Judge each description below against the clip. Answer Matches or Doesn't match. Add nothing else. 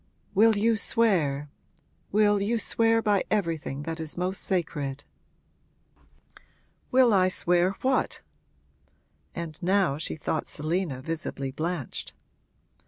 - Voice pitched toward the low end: Doesn't match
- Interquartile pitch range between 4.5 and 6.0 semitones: Matches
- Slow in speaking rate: Matches